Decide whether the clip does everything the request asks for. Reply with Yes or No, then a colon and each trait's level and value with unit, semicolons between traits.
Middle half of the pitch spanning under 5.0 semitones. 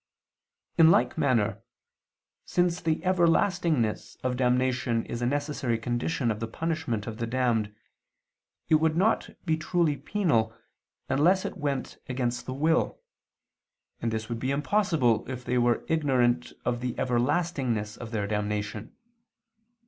No: wide, 5.4 semitones